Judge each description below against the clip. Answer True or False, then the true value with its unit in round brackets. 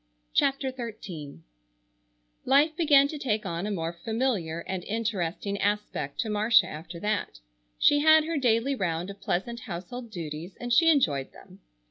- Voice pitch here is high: True (210 Hz)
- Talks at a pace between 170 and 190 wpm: False (150 wpm)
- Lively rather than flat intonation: True (7.2 semitones)